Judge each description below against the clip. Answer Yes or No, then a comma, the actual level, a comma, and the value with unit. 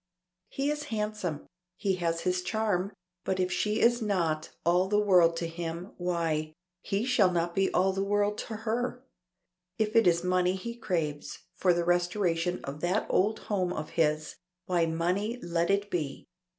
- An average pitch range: Yes, average, 3.7 semitones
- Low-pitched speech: No, medium, 180 Hz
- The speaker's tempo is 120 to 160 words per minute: No, average, 170 wpm